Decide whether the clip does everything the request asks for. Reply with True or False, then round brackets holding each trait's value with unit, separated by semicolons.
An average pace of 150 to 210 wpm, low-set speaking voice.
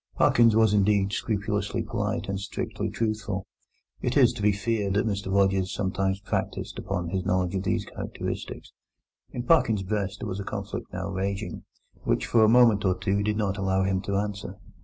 True (180 wpm; 100 Hz)